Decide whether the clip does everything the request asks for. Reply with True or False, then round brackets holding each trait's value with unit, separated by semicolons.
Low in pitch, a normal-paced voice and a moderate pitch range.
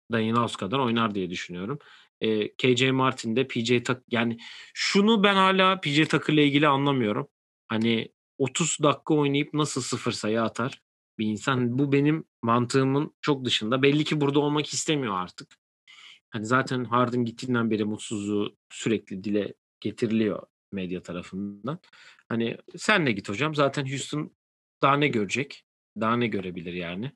False (125 Hz; 150 wpm; 4.8 semitones)